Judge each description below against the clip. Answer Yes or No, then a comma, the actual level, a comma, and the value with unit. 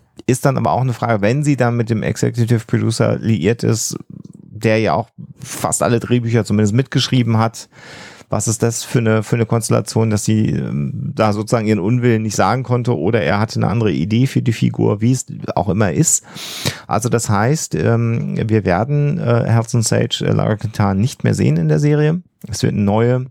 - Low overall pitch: Yes, low, 115 Hz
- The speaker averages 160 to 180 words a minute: No, fast, 190 wpm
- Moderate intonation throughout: Yes, average, 3.2 semitones